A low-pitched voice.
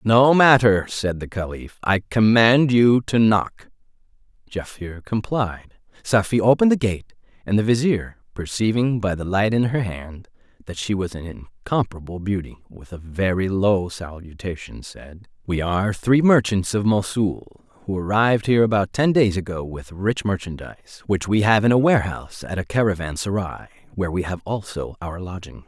Yes: low, 100 Hz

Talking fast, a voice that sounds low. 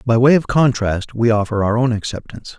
Yes: fast, 210 wpm; low, 120 Hz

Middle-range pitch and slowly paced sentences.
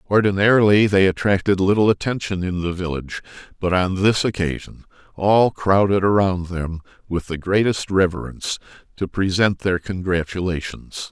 No: very low, 95 Hz; slow, 130 wpm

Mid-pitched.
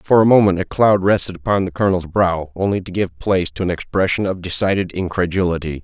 No: very low, 90 Hz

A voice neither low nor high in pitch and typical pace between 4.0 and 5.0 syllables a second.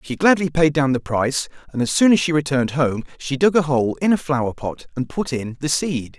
No: medium, 145 Hz; 5.6 syllables/s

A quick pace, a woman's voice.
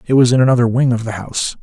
No: fast, 295 wpm; male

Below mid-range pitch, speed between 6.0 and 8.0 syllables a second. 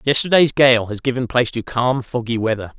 No: low, 125 Hz; 5.6 syllables/s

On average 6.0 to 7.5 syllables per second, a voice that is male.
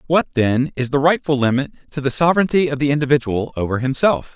Yes: 6.1 syllables/s; male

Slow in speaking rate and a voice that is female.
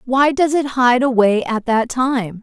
No: average, 200 wpm; female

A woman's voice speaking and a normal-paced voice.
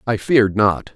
No: male; average, 190 wpm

